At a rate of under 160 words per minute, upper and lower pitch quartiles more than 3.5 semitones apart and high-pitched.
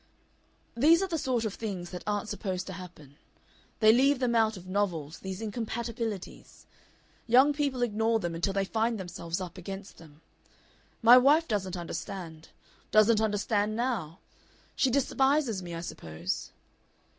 Yes: average, 145 wpm; average, 4.8 semitones; high, 210 Hz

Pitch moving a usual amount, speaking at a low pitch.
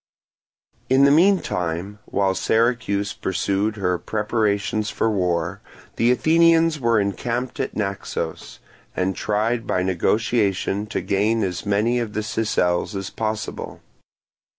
Yes: average, 3.2 semitones; low, 105 Hz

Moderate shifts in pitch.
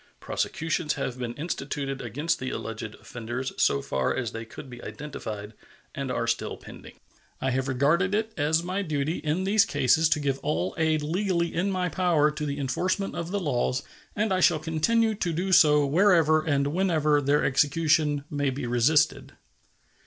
Yes: average, 4.4 semitones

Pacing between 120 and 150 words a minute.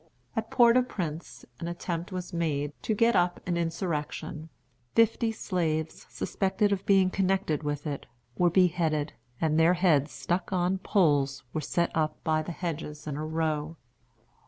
No: average, 160 wpm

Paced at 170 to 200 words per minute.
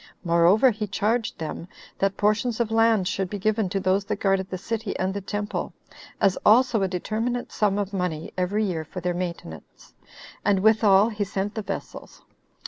Yes: average, 180 wpm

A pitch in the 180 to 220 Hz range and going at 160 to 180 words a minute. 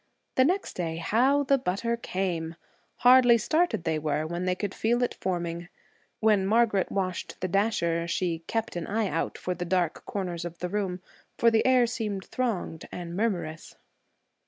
Yes: high, 190 Hz; average, 170 wpm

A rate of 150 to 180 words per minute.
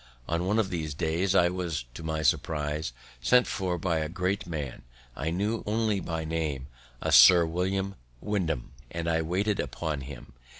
Yes: average, 170 wpm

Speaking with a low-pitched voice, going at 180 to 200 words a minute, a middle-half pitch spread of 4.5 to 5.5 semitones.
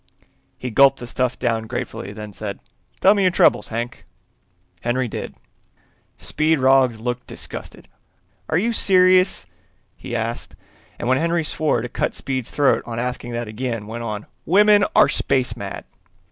No: low, 125 Hz; average, 155 wpm; average, 5.2 semitones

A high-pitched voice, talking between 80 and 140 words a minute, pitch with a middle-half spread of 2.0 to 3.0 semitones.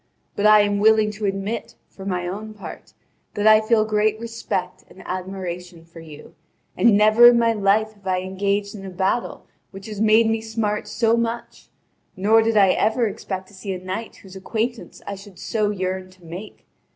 No: high, 205 Hz; average, 190 wpm; narrow, 2.6 semitones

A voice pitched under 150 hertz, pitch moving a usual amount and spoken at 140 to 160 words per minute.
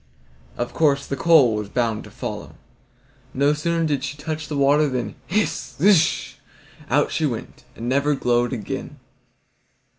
Yes: medium, 140 Hz; average, 4.0 semitones; average, 150 wpm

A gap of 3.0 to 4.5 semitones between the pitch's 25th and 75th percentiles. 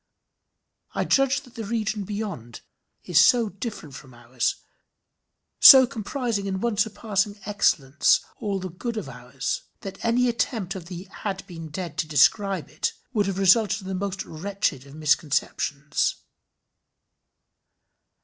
No: wide, 5.6 semitones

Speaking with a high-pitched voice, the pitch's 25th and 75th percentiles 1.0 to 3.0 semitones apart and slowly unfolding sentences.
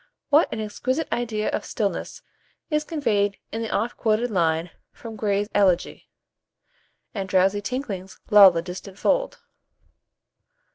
No: high, 210 Hz; average, 3.8 semitones; slow, 130 wpm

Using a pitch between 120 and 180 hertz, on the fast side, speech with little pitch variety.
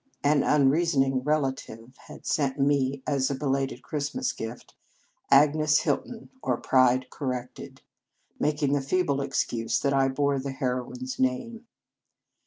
No: low, 135 Hz; average, 140 wpm; narrow, 2.2 semitones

